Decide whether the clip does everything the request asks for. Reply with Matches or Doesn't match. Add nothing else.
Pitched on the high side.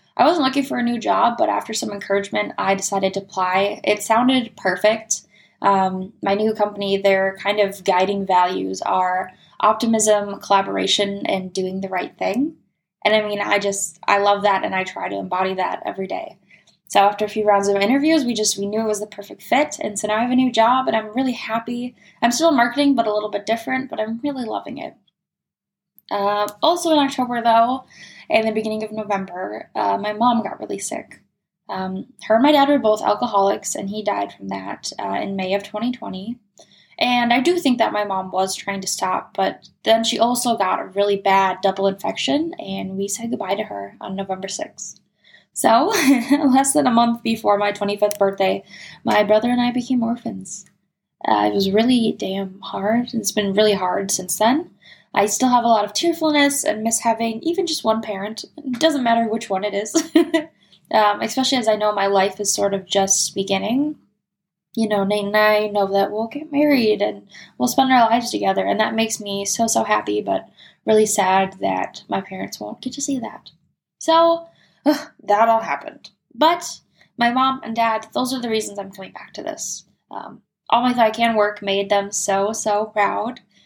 Matches